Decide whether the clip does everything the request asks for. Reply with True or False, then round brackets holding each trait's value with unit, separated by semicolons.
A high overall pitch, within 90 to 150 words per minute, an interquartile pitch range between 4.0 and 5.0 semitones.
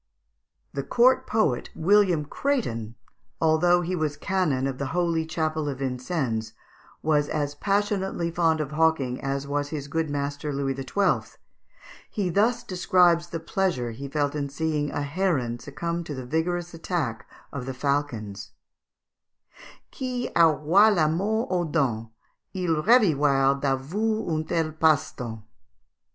False (155 Hz; 135 wpm; 4.3 semitones)